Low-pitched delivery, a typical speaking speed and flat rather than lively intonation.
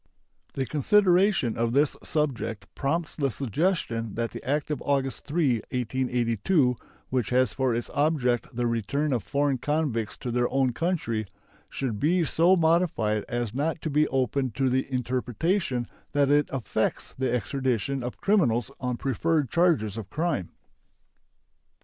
No: low, 130 Hz; average, 145 wpm; average, 4.1 semitones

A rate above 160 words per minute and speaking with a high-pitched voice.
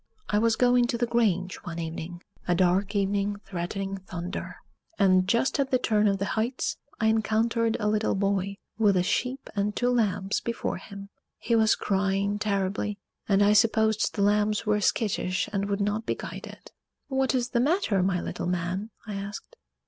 Yes: average, 180 wpm; high, 205 Hz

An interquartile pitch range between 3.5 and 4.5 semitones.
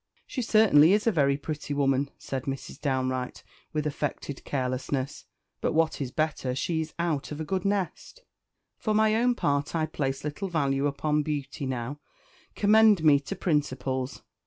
Yes: average, 3.9 semitones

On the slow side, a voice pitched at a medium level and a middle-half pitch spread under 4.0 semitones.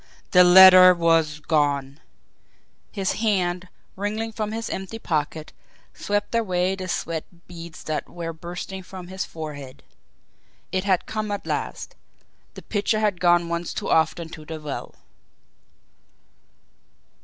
Yes: slow, 130 wpm; medium, 180 Hz; average, 3.4 semitones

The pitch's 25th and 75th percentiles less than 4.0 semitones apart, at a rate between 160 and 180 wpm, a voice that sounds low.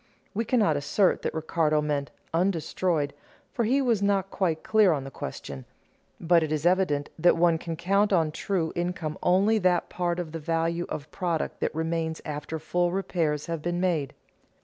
No: average, 3.1 semitones; average, 175 wpm; medium, 170 Hz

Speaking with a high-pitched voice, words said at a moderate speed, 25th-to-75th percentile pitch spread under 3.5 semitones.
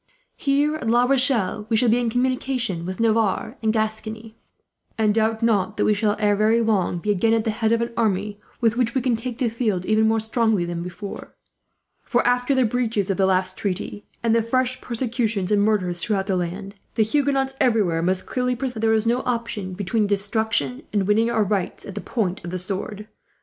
No: high, 220 Hz; fast, 210 wpm; average, 2.8 semitones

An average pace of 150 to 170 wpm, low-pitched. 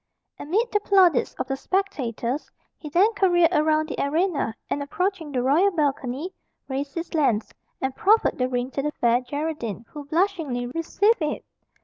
No: average, 160 wpm; very high, 300 Hz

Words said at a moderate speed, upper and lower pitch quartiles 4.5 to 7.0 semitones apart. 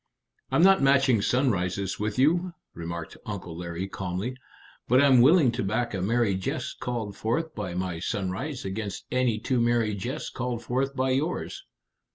Yes: average, 160 wpm; average, 5.3 semitones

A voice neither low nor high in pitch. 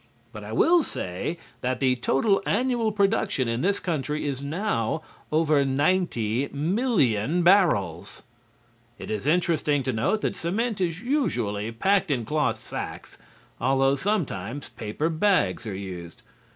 Yes: medium, 145 Hz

